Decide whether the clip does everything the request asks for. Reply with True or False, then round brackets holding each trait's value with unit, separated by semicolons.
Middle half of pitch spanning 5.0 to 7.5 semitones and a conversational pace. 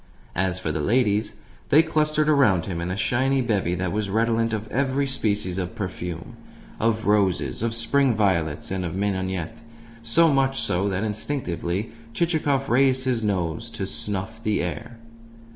True (5.6 semitones; 160 wpm)